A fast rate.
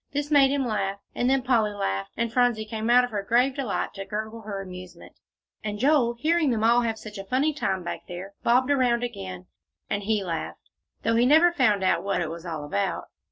Yes: fast, 215 wpm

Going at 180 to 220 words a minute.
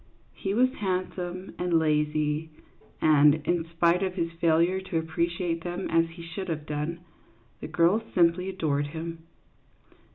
No: average, 140 wpm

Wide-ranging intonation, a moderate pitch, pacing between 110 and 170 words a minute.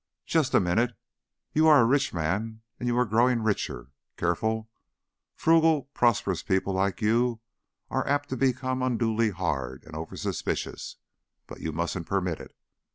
No: wide, 5.7 semitones; low, 110 Hz; average, 150 wpm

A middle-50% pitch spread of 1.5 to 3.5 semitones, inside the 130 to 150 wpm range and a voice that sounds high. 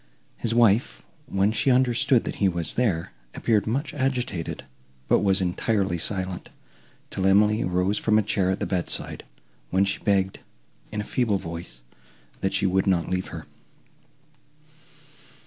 No: average, 3.0 semitones; average, 145 wpm; low, 100 Hz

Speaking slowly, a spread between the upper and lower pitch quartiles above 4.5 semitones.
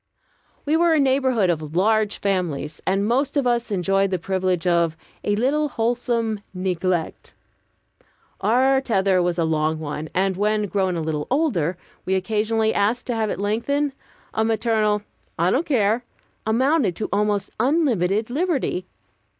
No: average, 150 wpm; average, 5.0 semitones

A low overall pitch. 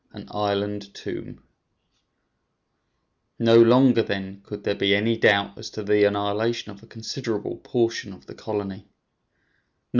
Yes: low, 105 Hz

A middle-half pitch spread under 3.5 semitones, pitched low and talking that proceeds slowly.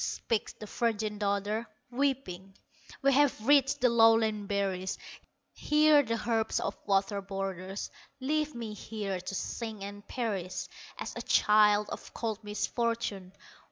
No: average, 2.9 semitones; high, 215 Hz; slow, 130 wpm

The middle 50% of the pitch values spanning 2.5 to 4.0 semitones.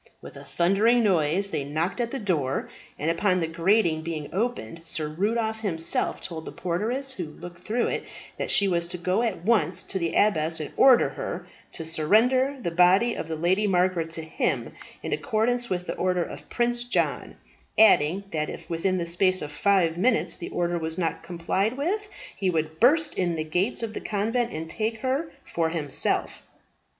No: average, 5.3 semitones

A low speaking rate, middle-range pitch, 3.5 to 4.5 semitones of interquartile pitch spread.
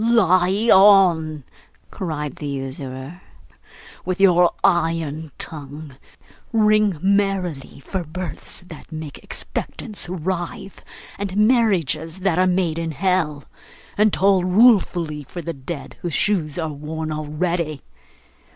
Yes: slow, 115 wpm; medium, 175 Hz; average, 3.9 semitones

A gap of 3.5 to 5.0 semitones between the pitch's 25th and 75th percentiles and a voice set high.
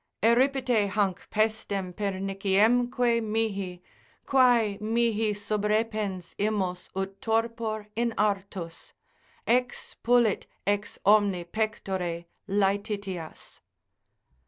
No: average, 2.7 semitones; high, 210 Hz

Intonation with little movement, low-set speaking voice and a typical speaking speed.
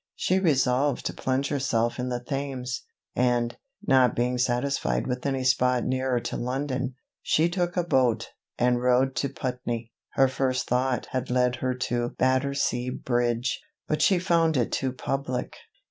Yes: narrow, 1.7 semitones; low, 130 Hz; average, 155 wpm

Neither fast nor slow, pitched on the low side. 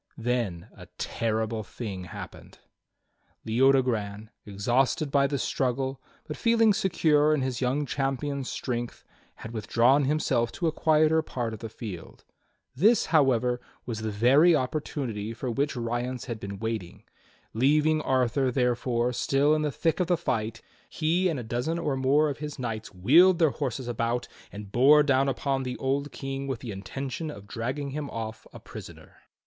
Yes: average, 160 wpm; low, 130 Hz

